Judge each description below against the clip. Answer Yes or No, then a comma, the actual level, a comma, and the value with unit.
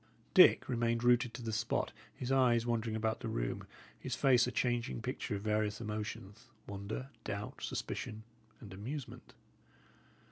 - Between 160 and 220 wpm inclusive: No, average, 145 wpm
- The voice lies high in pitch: No, low, 115 Hz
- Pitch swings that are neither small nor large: No, narrow, 2.3 semitones